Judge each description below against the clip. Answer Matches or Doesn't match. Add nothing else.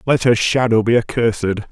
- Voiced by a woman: Doesn't match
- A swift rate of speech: Doesn't match